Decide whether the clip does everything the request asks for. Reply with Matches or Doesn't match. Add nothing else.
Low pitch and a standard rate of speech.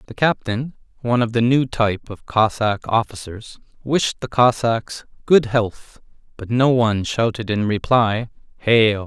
Doesn't match